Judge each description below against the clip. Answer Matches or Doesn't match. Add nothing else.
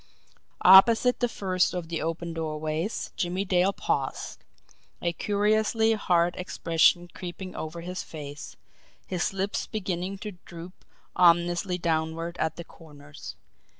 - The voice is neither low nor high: Matches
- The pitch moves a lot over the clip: Doesn't match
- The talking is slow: Matches